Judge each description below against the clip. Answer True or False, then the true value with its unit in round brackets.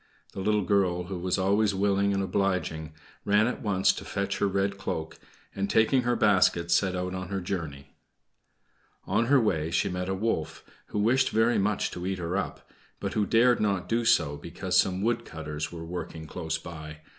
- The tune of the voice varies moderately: True (3.2 semitones)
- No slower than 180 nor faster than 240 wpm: True (190 wpm)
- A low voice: True (95 Hz)